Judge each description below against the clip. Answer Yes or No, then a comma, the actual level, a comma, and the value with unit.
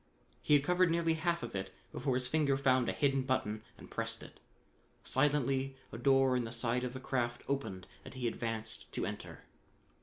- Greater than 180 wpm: Yes, average, 190 wpm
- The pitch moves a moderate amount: Yes, average, 3.0 semitones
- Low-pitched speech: Yes, low, 130 Hz